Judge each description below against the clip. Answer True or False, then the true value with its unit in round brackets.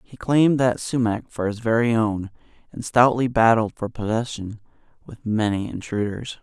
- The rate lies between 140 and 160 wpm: True (150 wpm)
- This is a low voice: True (115 Hz)